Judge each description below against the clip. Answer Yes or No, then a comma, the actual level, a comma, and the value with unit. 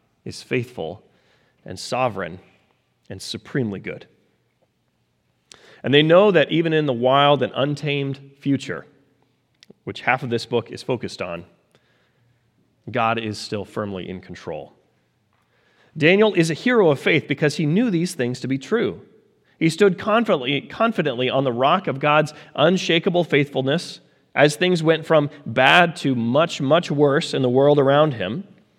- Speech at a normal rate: Yes, average, 150 wpm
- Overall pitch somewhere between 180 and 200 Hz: No, medium, 140 Hz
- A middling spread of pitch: Yes, average, 4.7 semitones